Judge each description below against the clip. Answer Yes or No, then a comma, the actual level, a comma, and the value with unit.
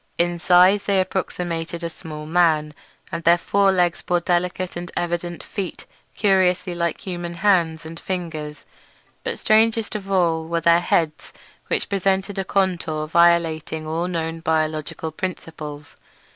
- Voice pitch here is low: No, medium, 170 Hz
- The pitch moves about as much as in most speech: No, narrow, 2.3 semitones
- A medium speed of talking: Yes, average, 145 wpm